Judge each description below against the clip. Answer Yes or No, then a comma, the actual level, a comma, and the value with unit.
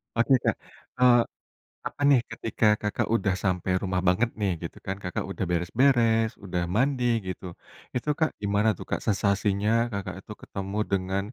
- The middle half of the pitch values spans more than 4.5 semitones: No, average, 3.3 semitones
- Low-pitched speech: Yes, low, 100 Hz